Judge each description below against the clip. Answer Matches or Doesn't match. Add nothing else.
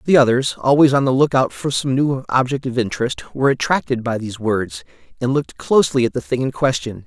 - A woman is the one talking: Doesn't match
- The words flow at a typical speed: Doesn't match